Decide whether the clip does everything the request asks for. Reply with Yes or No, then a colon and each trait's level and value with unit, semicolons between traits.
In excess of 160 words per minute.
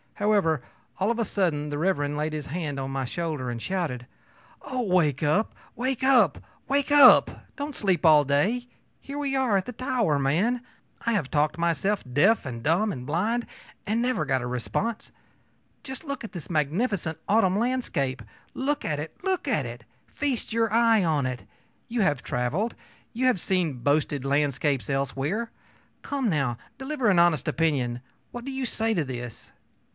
Yes: average, 170 wpm